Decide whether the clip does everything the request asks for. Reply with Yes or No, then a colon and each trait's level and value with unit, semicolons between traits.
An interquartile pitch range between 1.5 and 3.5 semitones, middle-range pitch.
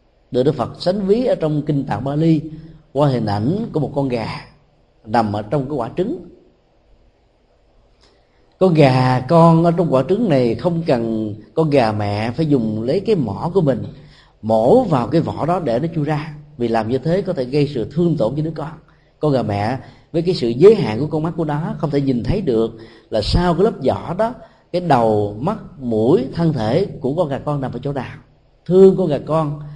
No: average, 4.8 semitones; medium, 145 Hz